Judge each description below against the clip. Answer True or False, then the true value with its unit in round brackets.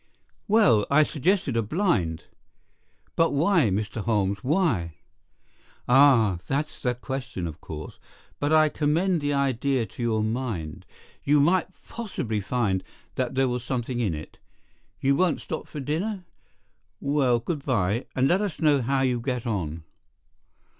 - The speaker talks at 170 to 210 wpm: False (145 wpm)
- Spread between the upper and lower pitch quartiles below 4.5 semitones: False (5.4 semitones)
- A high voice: False (130 Hz)